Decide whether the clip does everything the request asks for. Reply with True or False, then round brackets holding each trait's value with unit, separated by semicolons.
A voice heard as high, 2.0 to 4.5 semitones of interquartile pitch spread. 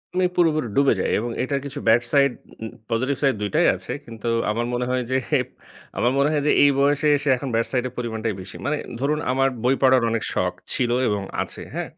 False (130 Hz; 3.5 semitones)